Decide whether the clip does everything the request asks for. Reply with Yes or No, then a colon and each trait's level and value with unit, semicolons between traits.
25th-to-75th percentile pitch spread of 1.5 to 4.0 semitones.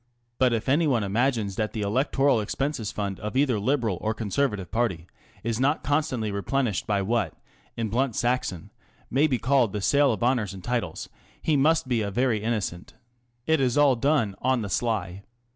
No: average, 4.5 semitones